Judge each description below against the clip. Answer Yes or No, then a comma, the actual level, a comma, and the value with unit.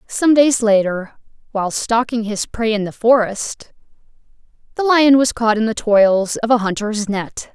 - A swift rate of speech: No, average, 165 wpm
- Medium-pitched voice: No, high, 225 Hz